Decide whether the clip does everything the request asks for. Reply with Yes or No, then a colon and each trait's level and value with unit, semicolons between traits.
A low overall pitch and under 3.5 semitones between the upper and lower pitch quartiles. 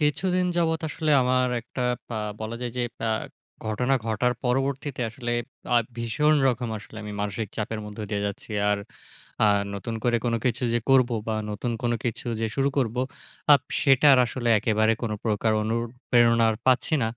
Yes: low, 120 Hz; average, 2.8 semitones